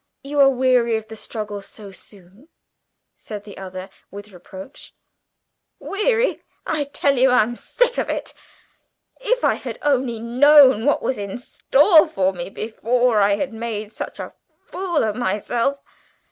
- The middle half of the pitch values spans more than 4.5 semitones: Yes, average, 5.3 semitones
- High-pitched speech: Yes, high, 235 Hz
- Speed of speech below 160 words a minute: Yes, average, 150 wpm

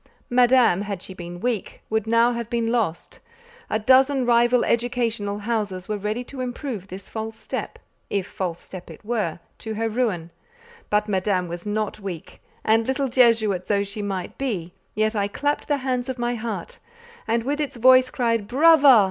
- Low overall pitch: No, high, 225 Hz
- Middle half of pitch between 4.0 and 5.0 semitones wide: No, average, 3.5 semitones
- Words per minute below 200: Yes, average, 170 wpm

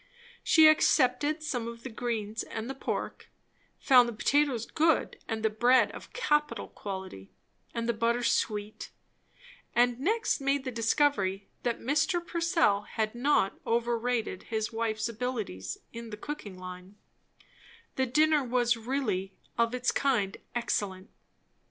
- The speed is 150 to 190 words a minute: No, slow, 135 wpm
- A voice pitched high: Yes, high, 235 Hz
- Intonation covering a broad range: No, average, 3.9 semitones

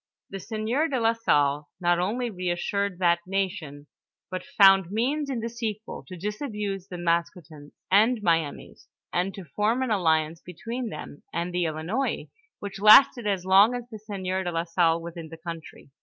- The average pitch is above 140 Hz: Yes, high, 190 Hz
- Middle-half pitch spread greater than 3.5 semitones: Yes, average, 4.4 semitones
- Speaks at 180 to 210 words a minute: No, average, 170 wpm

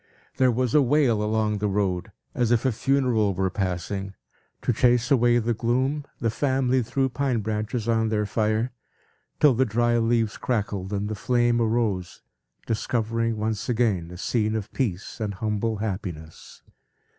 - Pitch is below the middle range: Yes, low, 110 Hz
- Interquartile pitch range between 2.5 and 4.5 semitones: Yes, average, 2.8 semitones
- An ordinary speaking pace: Yes, average, 155 wpm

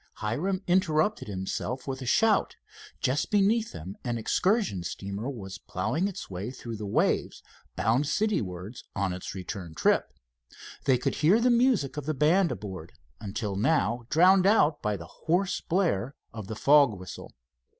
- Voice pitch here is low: Yes, low, 130 Hz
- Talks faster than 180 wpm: No, average, 150 wpm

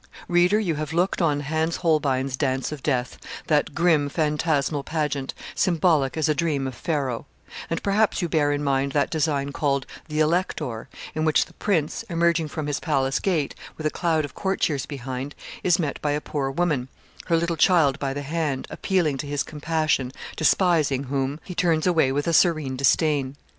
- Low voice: No, medium, 150 Hz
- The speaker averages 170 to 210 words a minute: Yes, average, 180 wpm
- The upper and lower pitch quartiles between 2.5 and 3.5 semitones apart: Yes, average, 3.1 semitones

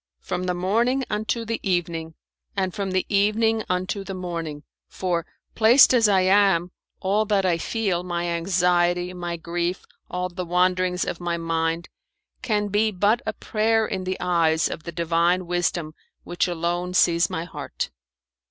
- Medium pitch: Yes, medium, 180 Hz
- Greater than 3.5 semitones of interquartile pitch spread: No, average, 2.8 semitones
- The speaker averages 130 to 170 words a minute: Yes, average, 160 wpm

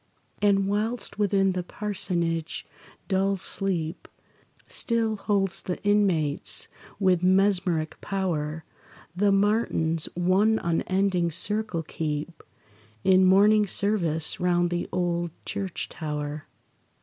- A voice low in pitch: No, medium, 185 Hz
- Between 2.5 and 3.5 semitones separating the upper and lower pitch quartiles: Yes, average, 3.1 semitones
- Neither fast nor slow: No, slow, 100 wpm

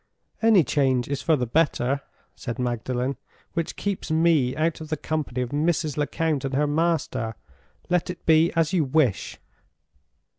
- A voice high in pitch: No, medium, 150 Hz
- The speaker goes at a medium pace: Yes, average, 155 wpm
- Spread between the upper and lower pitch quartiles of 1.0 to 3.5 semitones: No, average, 4.0 semitones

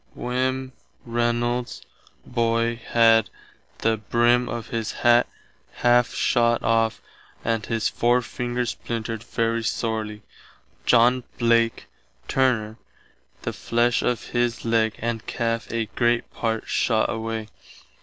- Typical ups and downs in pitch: No, narrow, 1.1 semitones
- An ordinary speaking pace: No, slow, 110 wpm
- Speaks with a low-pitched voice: Yes, low, 115 Hz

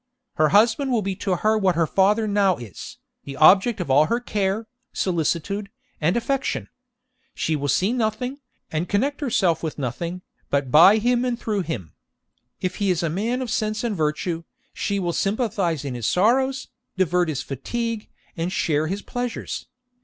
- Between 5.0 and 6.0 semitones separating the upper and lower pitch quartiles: Yes, wide, 5.5 semitones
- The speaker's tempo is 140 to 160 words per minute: No, average, 170 wpm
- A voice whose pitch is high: Yes, high, 195 Hz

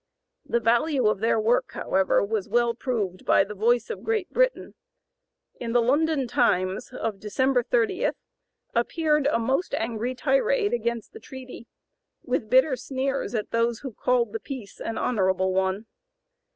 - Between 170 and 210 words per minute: No, average, 150 wpm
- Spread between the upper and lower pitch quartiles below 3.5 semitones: No, average, 3.8 semitones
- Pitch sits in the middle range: No, high, 240 Hz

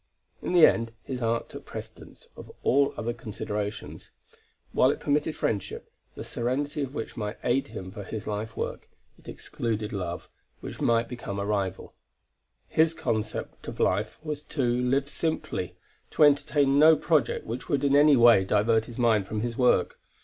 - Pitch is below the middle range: Yes, low, 120 Hz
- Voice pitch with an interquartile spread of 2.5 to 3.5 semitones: No, average, 4.9 semitones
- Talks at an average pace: Yes, average, 170 wpm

